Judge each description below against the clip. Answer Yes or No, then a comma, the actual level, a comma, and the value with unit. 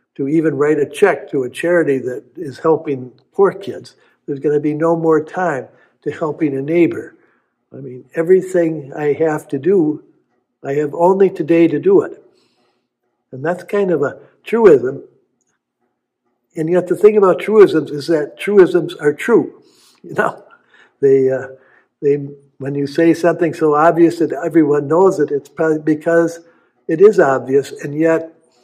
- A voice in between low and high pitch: Yes, medium, 160 Hz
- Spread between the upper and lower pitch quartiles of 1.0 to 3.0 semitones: No, average, 3.4 semitones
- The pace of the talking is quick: No, average, 165 wpm